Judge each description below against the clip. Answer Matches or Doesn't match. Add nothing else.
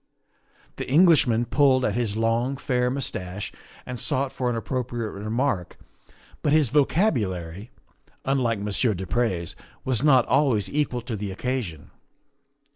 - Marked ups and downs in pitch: Doesn't match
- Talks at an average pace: Doesn't match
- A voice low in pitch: Matches